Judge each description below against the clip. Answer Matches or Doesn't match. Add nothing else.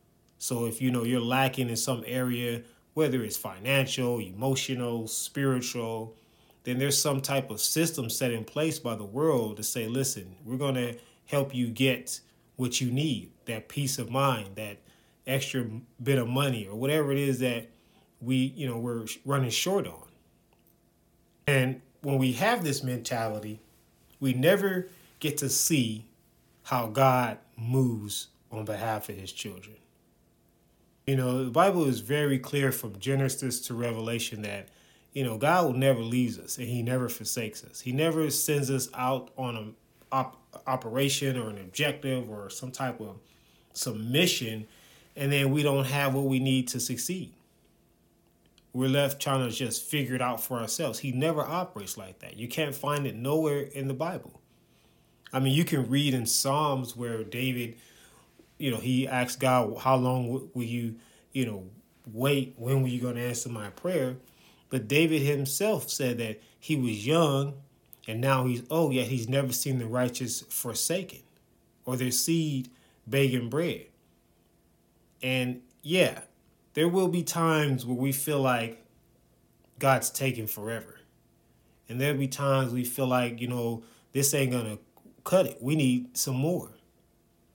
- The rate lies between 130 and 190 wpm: Matches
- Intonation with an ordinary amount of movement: Matches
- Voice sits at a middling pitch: Doesn't match